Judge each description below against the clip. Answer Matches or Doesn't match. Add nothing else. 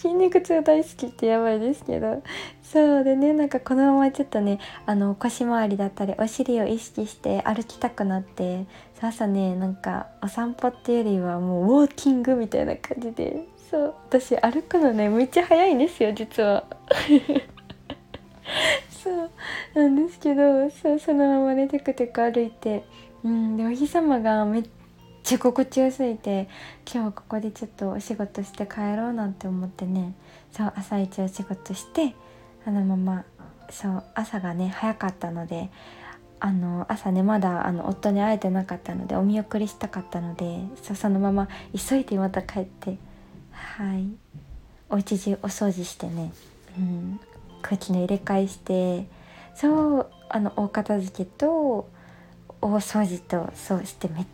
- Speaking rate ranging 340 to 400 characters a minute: Doesn't match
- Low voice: Doesn't match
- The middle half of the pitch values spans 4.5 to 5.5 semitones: Matches